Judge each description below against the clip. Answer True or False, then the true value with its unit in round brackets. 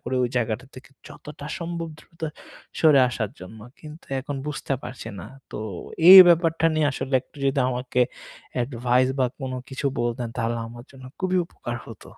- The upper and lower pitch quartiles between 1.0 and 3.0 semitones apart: False (3.8 semitones)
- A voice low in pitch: True (130 Hz)